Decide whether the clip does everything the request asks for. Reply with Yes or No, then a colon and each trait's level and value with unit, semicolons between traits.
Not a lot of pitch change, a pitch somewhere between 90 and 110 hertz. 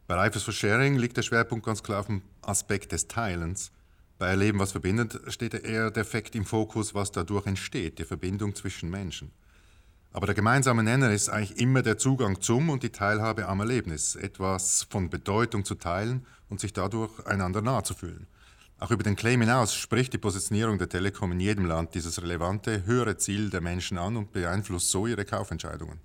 No: average, 3.4 semitones; low, 100 Hz